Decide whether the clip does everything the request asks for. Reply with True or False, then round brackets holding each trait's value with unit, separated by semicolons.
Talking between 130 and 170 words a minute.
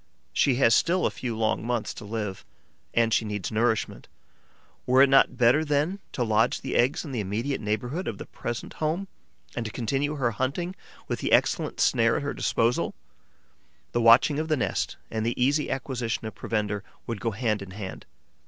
False (190 wpm)